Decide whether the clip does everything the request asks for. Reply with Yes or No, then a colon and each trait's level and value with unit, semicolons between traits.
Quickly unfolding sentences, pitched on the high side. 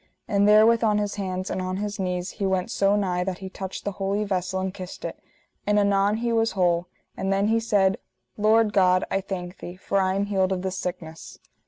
Yes: fast, 220 wpm; high, 195 Hz